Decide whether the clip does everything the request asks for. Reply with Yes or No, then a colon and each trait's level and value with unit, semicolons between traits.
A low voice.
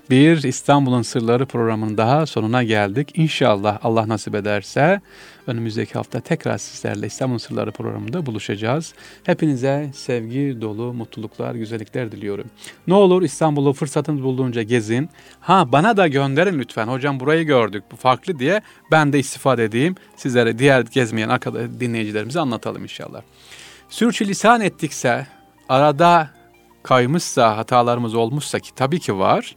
Yes: low, 130 Hz